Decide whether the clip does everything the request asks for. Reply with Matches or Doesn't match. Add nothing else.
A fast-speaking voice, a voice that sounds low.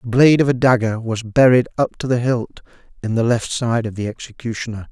Matches